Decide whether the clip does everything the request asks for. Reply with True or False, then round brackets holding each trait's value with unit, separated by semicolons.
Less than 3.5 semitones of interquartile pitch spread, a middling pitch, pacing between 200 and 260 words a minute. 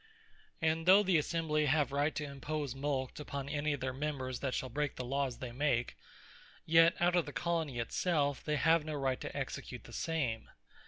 True (3.0 semitones; 145 Hz; 205 wpm)